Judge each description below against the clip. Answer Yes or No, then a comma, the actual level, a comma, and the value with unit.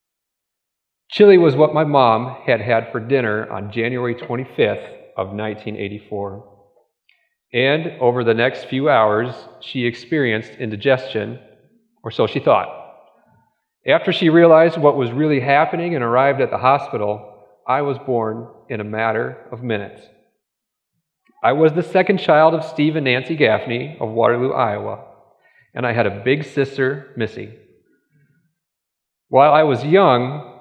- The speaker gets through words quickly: No, average, 140 wpm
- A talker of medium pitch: No, low, 130 Hz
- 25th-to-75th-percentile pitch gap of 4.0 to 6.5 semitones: Yes, wide, 5.5 semitones